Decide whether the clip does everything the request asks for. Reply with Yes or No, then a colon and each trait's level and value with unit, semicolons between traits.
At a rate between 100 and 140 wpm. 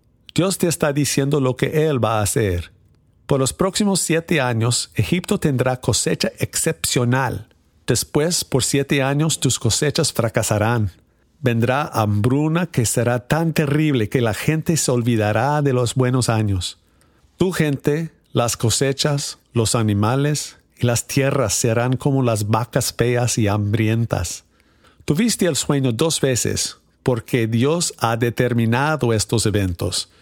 Yes: slow, 135 wpm